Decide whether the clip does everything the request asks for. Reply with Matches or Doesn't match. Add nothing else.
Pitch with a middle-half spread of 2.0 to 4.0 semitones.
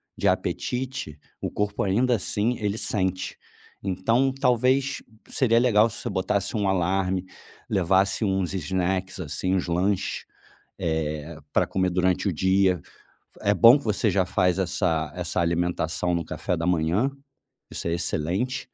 Matches